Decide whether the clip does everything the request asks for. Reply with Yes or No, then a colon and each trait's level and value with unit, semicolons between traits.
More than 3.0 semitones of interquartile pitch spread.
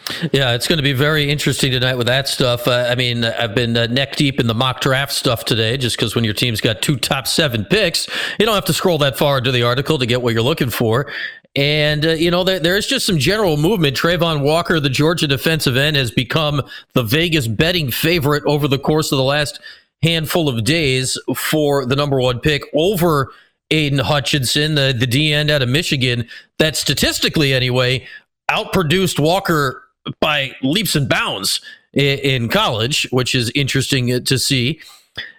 Yes: average, 3.6 semitones